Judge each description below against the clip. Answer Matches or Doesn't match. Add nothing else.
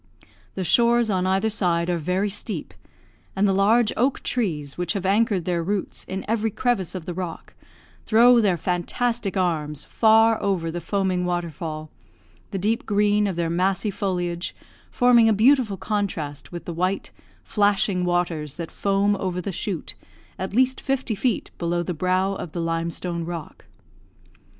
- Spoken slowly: Doesn't match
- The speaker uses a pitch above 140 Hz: Matches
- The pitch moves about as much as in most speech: Matches